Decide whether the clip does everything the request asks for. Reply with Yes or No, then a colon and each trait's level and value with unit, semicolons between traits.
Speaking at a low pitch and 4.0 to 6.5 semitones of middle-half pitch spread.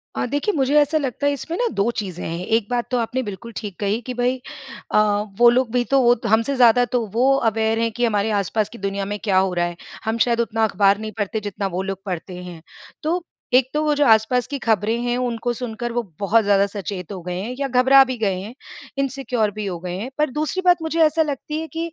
No: high, 230 Hz; average, 4.4 semitones